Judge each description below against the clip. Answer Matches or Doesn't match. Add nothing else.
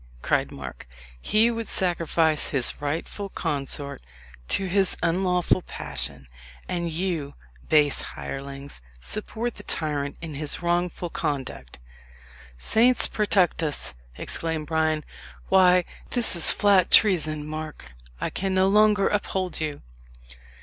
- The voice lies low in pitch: Doesn't match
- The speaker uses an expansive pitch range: Doesn't match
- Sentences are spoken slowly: Matches